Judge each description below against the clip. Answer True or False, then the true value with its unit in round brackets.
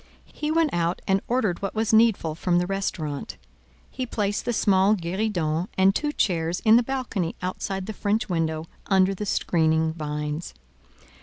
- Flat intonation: False (4.6 semitones)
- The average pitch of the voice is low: False (190 Hz)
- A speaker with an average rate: True (160 wpm)